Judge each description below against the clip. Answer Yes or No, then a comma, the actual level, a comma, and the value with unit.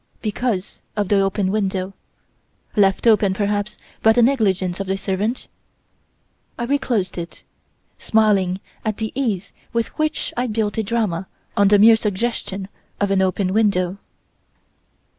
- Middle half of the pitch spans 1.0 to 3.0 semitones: Yes, narrow, 2.6 semitones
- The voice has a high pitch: Yes, high, 205 Hz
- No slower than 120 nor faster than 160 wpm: Yes, average, 140 wpm